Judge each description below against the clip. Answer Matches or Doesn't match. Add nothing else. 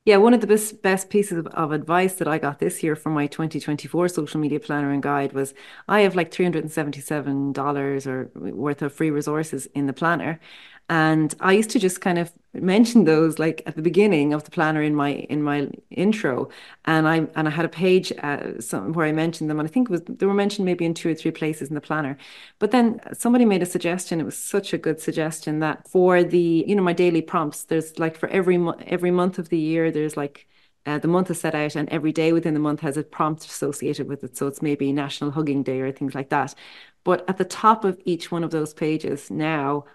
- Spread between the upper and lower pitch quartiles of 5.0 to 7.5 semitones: Doesn't match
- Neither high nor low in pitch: Matches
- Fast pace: Matches